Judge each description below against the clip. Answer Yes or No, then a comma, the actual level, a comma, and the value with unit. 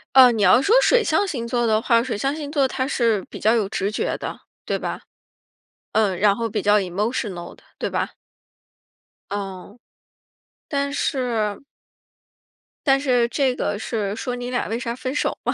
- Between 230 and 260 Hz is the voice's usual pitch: Yes, high, 235 Hz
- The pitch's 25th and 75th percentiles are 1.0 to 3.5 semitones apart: No, average, 4.0 semitones